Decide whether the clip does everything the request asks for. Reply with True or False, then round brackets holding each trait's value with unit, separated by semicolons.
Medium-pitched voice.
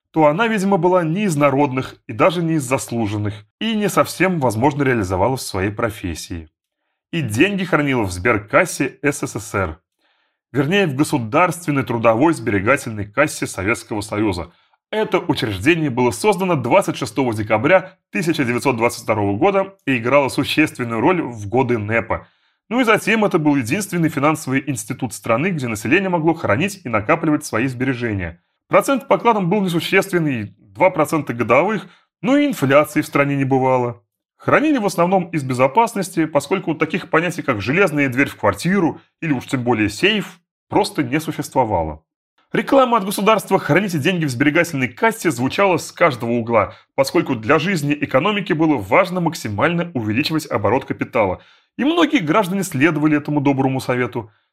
True (145 Hz)